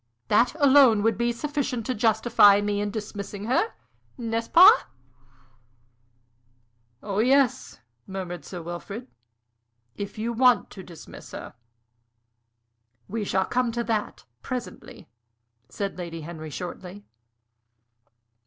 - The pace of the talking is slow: Yes, slow, 115 wpm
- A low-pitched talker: No, high, 215 Hz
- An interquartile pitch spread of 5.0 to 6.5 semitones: No, average, 3.7 semitones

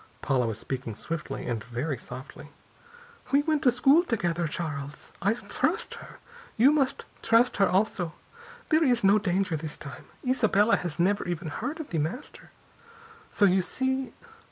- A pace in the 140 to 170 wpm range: Yes, average, 155 wpm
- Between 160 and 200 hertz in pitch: Yes, high, 190 Hz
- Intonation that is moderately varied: No, wide, 8.5 semitones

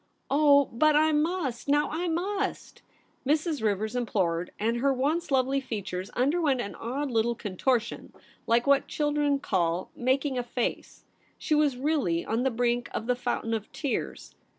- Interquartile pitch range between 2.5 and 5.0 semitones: Yes, average, 4.5 semitones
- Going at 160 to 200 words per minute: Yes, average, 165 wpm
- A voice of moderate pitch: No, very high, 260 Hz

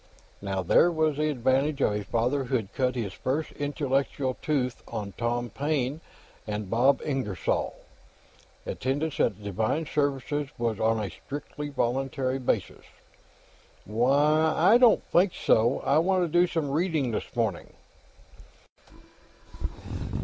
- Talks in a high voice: No, low, 135 Hz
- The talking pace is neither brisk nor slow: No, slow, 130 wpm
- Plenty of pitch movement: No, average, 4.4 semitones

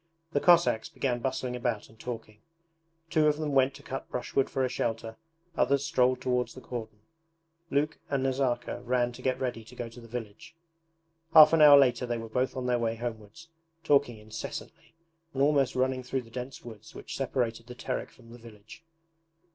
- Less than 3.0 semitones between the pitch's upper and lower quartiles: Yes, narrow, 2.6 semitones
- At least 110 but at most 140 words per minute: No, average, 185 wpm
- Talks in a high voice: No, low, 125 Hz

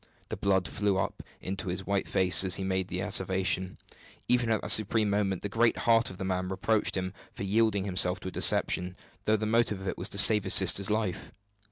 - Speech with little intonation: Yes, narrow, 2.2 semitones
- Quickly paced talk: Yes, fast, 220 wpm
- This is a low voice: Yes, very low, 95 Hz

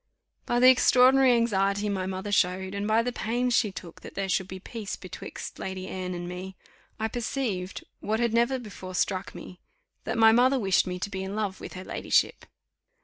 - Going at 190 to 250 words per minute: Yes, average, 200 wpm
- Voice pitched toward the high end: Yes, high, 200 Hz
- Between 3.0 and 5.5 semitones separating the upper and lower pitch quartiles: Yes, average, 3.9 semitones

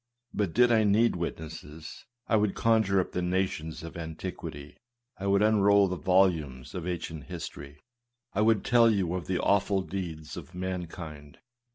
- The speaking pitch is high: No, very low, 90 Hz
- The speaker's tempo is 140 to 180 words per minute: Yes, average, 165 wpm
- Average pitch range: Yes, average, 3.8 semitones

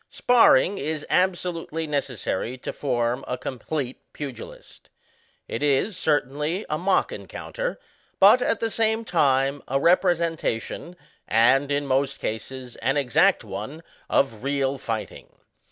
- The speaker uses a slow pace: Yes, slow, 125 wpm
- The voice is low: No, medium, 145 Hz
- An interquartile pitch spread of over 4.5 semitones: Yes, average, 4.9 semitones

